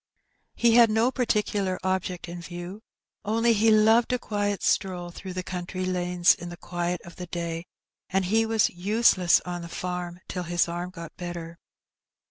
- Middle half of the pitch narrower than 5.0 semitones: Yes, average, 3.4 semitones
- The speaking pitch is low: No, medium, 180 Hz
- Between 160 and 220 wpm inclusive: Yes, average, 170 wpm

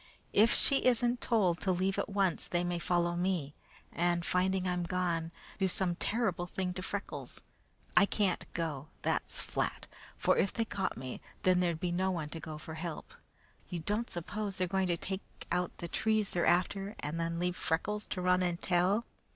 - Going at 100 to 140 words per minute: No, average, 190 wpm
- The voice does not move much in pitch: Yes, narrow, 2.2 semitones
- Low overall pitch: No, medium, 180 Hz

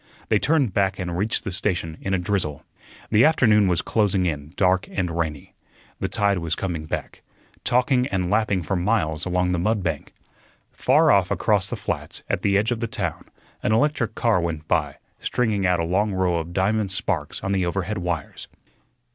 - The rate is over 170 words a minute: Yes, average, 190 wpm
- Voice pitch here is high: No, very low, 95 Hz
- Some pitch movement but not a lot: Yes, average, 3.6 semitones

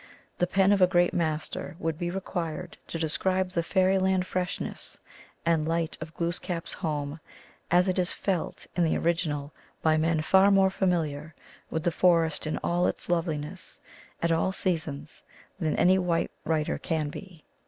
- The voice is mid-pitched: Yes, medium, 170 Hz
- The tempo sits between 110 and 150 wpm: No, average, 165 wpm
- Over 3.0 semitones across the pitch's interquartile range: No, narrow, 2.6 semitones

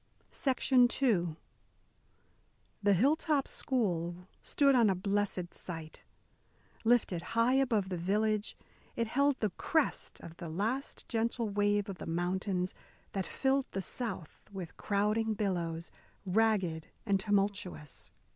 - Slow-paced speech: Yes, slow, 120 wpm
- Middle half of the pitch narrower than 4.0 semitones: No, average, 4.3 semitones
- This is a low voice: No, high, 205 Hz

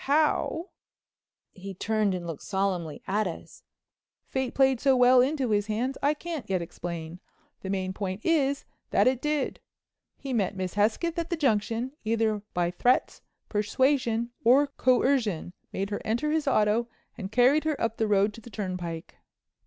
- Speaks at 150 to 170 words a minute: Yes, average, 160 wpm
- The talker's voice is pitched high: Yes, high, 225 Hz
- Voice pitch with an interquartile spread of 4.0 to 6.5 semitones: Yes, wide, 5.5 semitones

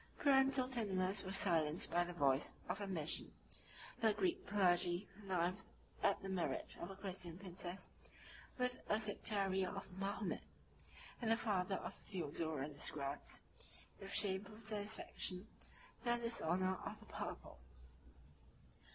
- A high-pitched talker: Yes, high, 195 Hz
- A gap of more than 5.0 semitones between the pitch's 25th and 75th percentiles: No, average, 3.3 semitones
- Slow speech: Yes, slow, 125 wpm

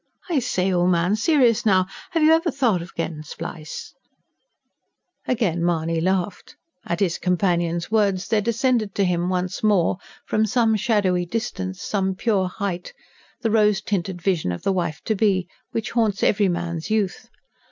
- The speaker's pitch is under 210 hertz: Yes, high, 190 Hz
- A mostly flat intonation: No, average, 3.7 semitones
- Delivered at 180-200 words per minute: No, average, 160 wpm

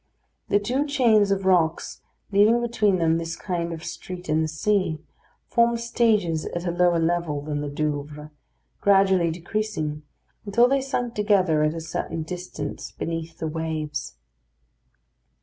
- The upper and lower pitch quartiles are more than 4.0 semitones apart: Yes, average, 4.7 semitones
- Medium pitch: Yes, medium, 175 Hz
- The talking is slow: No, average, 145 wpm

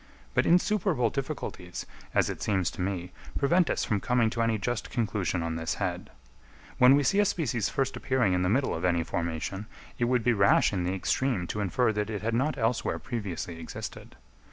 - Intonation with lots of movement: Yes, wide, 5.8 semitones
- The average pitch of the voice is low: Yes, low, 110 Hz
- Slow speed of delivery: No, average, 200 wpm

